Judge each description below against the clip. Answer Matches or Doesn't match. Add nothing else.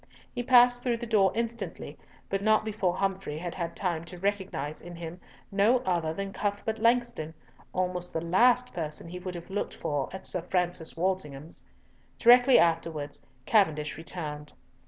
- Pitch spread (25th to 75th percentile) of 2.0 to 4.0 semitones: Doesn't match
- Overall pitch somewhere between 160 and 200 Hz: Matches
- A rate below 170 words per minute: Matches